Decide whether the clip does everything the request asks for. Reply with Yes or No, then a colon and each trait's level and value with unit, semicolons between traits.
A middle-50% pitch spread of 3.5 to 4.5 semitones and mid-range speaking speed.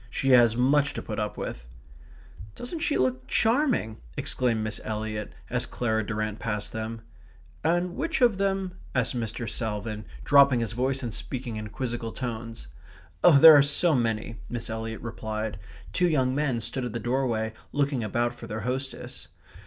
Yes: average, 3.9 semitones; average, 165 wpm